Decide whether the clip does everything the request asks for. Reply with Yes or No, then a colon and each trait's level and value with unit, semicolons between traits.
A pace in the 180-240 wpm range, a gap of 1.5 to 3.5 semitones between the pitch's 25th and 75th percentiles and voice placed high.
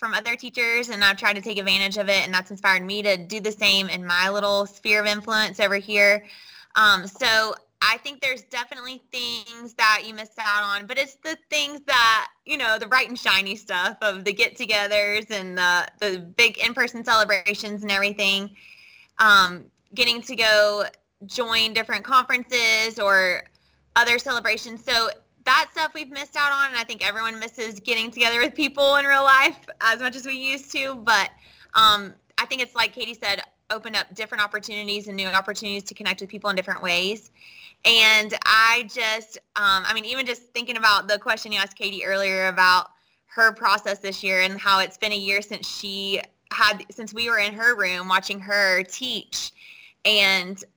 Yes: average, 190 wpm; average, 3.0 semitones; high, 215 Hz